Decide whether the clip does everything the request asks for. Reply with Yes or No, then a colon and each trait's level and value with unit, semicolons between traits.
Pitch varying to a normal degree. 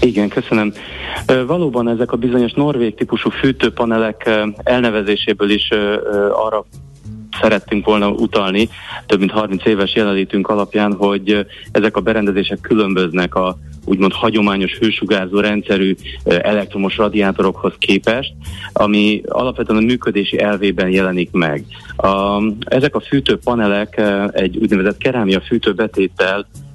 No: narrow, 2.3 semitones